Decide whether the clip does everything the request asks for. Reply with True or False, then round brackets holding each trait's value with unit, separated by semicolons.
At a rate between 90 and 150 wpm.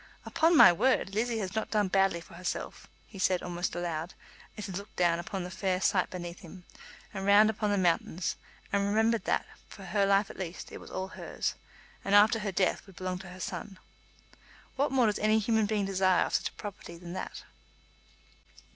False (200 wpm)